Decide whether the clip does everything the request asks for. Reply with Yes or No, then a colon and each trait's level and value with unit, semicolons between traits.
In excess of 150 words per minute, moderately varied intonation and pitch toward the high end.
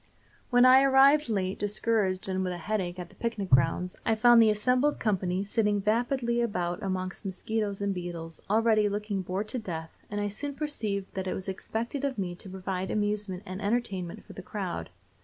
Yes: average, 190 wpm; average, 3.6 semitones; high, 205 Hz